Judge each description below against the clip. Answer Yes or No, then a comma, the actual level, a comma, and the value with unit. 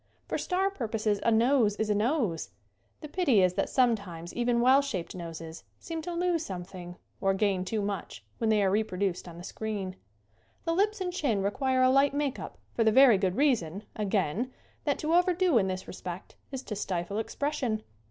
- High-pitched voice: Yes, high, 220 Hz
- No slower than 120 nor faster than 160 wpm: No, average, 190 wpm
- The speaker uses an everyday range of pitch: No, wide, 6.6 semitones